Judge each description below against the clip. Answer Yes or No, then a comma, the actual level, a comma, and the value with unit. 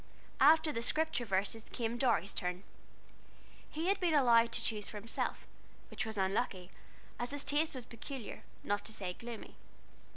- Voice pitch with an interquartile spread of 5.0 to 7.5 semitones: Yes, wide, 5.6 semitones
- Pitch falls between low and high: No, high, 230 Hz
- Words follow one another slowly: No, average, 160 wpm